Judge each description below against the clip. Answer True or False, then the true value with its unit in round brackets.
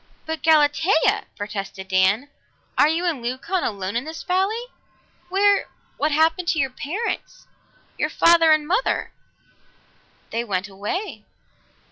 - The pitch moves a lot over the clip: True (7.7 semitones)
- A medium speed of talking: False (125 wpm)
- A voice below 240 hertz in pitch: False (310 Hz)